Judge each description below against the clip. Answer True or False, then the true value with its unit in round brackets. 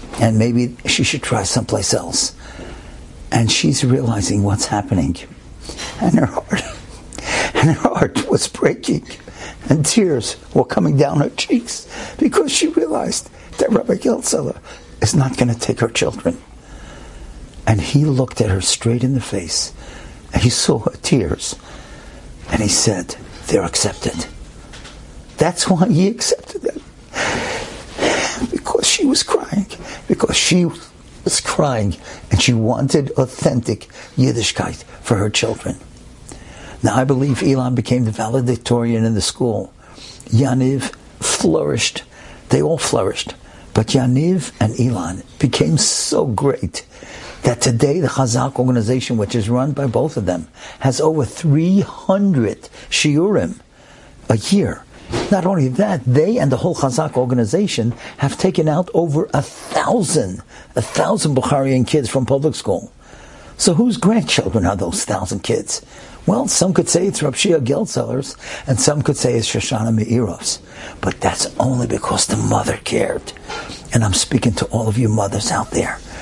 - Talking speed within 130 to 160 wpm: True (140 wpm)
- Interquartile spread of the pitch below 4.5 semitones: False (5.2 semitones)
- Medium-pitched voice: False (130 Hz)